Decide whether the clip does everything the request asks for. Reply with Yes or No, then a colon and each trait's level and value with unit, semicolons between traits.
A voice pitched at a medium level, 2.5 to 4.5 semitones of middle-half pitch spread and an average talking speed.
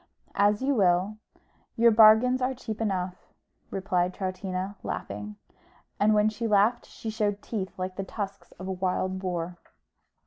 No: high, 200 Hz; average, 2.8 semitones; average, 145 wpm